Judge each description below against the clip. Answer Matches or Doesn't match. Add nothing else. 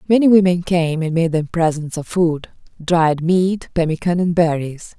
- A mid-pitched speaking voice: Matches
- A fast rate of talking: Doesn't match